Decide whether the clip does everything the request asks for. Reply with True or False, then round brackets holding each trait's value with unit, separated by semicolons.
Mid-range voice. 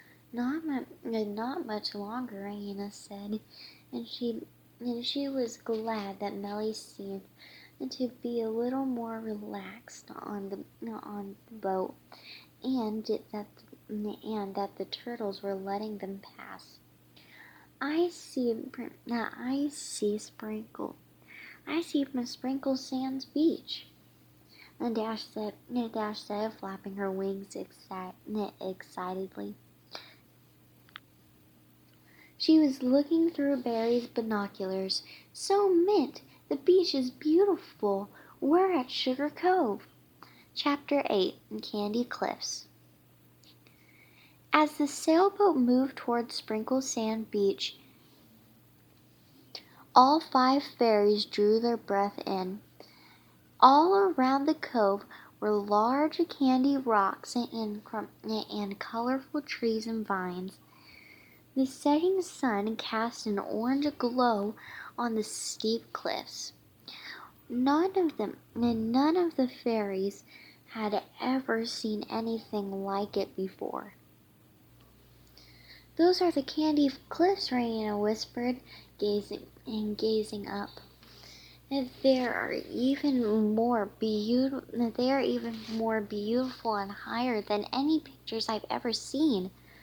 False (225 Hz)